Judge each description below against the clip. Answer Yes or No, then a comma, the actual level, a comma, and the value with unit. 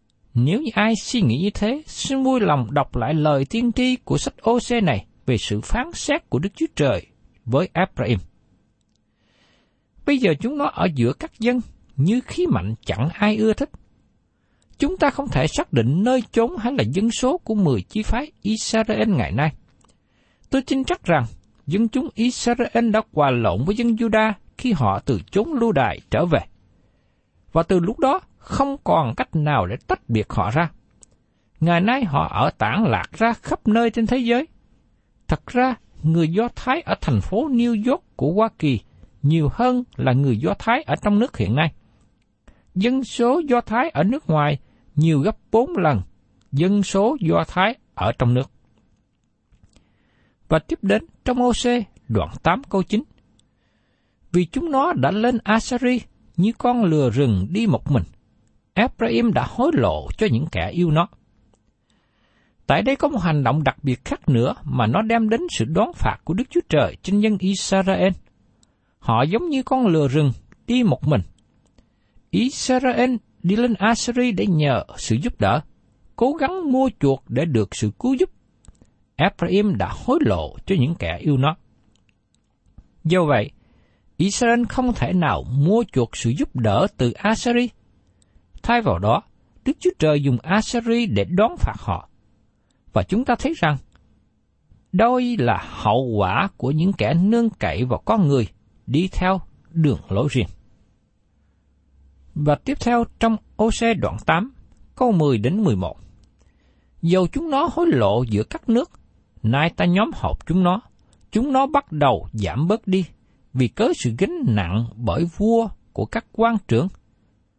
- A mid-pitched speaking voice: Yes, medium, 170 Hz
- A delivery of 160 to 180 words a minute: Yes, average, 170 wpm